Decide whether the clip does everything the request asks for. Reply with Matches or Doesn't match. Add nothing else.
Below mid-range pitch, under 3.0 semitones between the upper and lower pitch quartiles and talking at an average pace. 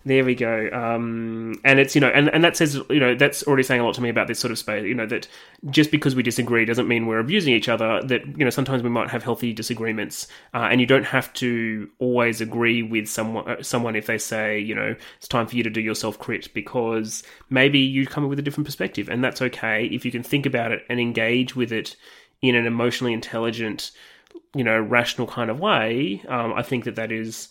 Doesn't match